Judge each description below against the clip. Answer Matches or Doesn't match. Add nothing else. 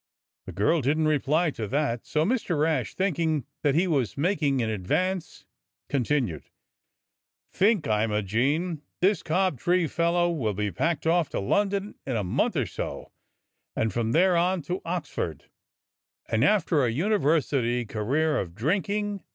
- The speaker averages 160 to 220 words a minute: Doesn't match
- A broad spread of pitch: Matches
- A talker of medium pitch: Matches